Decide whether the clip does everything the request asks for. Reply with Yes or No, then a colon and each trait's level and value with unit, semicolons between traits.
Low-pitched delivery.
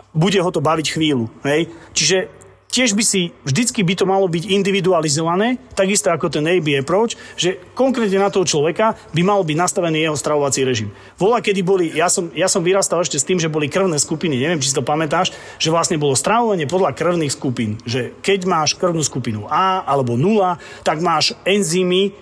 No: medium, 175 Hz